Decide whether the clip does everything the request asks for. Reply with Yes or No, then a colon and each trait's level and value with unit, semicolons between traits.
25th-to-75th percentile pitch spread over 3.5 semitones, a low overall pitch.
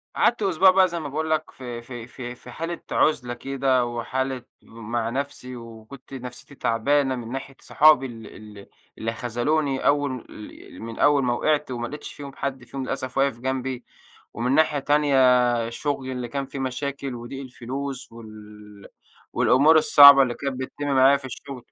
No: average, 2.8 semitones; low, 130 Hz